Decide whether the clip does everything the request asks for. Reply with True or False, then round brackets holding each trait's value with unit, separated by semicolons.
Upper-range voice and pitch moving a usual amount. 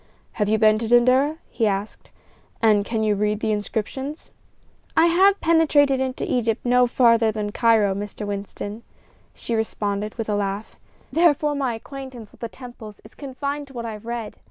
True (230 Hz; 3.9 semitones)